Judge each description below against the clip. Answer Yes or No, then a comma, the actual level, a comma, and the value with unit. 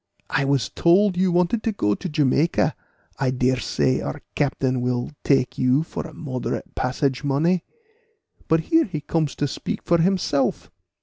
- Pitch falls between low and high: Yes, medium, 145 Hz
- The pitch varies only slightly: No, average, 4.9 semitones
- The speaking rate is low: No, average, 165 wpm